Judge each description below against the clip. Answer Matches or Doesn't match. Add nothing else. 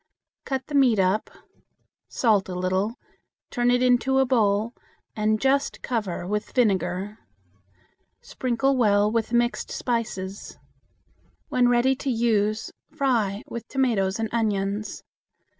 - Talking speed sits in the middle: Doesn't match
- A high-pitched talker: Matches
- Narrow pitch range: Doesn't match